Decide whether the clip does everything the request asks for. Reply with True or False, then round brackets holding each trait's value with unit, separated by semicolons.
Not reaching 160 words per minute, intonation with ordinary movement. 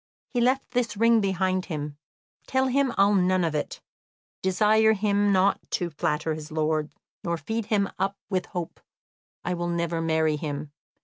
False (165 wpm; 4.8 semitones)